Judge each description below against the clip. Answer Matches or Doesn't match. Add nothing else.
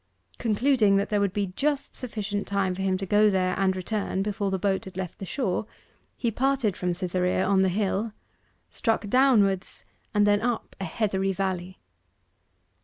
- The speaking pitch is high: Matches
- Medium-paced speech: Matches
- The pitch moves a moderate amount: Doesn't match